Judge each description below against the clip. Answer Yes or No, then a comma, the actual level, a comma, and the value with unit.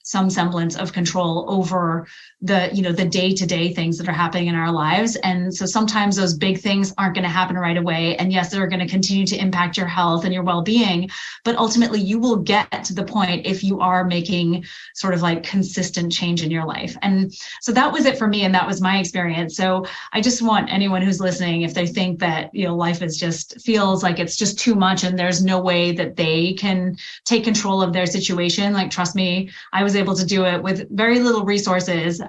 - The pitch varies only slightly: Yes, narrow, 1.8 semitones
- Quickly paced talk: Yes, fast, 225 wpm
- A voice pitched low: No, medium, 185 Hz